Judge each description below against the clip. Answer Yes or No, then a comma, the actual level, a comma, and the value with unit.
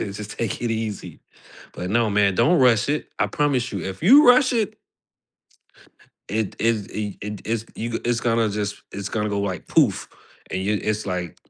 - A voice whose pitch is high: No, low, 110 Hz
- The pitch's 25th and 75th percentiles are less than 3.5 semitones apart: Yes, average, 2.8 semitones